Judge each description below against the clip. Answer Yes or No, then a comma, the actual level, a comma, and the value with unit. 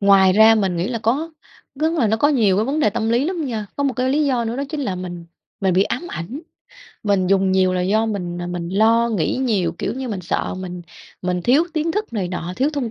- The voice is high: Yes, high, 220 Hz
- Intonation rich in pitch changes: Yes, wide, 6.0 semitones